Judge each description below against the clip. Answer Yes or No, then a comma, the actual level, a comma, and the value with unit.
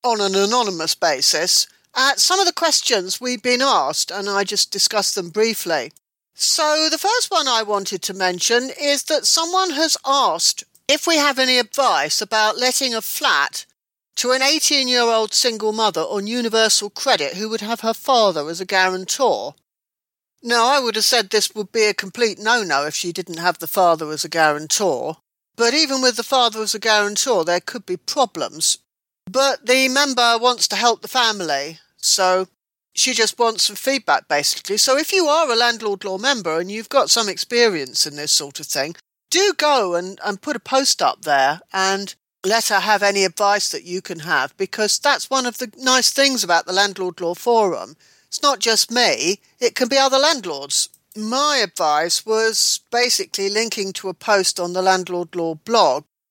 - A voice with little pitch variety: No, wide, 5.6 semitones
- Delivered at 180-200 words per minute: Yes, average, 190 wpm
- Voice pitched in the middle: No, high, 220 Hz